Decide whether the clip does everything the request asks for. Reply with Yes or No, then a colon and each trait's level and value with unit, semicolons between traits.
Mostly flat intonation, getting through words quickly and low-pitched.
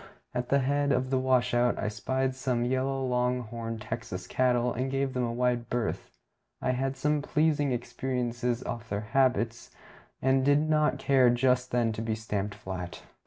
No: narrow, 2.2 semitones; average, 175 wpm; low, 125 Hz